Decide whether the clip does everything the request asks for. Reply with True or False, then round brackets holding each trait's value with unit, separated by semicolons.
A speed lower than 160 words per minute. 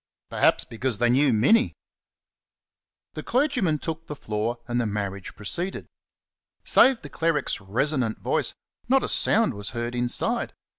True (140 wpm)